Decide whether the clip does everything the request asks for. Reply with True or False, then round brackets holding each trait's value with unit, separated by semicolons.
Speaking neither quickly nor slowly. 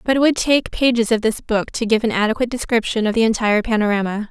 False (235 wpm)